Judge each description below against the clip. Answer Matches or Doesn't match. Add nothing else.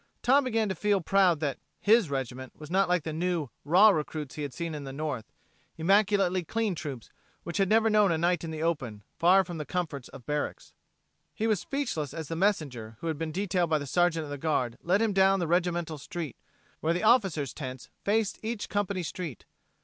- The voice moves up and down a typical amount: Matches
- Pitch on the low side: Doesn't match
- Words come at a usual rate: Doesn't match